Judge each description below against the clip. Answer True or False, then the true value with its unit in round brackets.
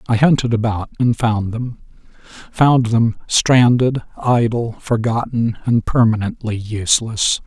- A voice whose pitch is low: True (115 Hz)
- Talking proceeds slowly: True (105 wpm)